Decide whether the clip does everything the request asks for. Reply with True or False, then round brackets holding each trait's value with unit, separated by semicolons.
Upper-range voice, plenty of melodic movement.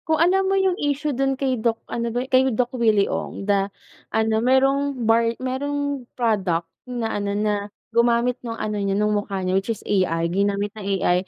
False (230 Hz; 4.5 semitones)